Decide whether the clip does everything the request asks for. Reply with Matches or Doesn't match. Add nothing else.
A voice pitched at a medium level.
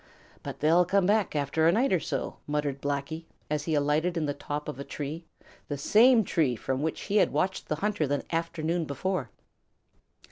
Matches